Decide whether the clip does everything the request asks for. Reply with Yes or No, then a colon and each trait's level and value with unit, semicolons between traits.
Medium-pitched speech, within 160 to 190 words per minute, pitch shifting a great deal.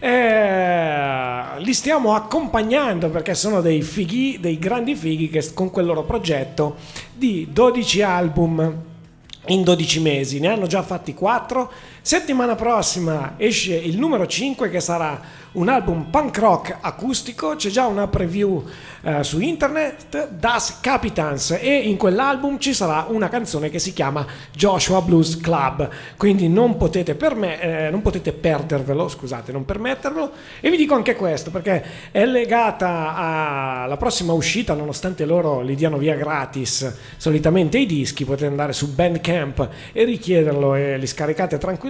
No: medium, 175 Hz; average, 150 wpm; wide, 6.4 semitones